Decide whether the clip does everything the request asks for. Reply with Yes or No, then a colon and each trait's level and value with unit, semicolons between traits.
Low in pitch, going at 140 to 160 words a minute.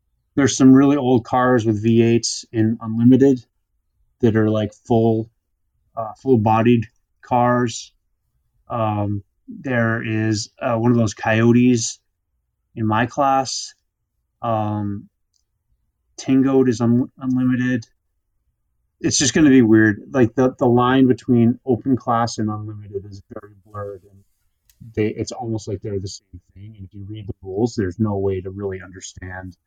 Yes: low, 110 Hz; average, 145 wpm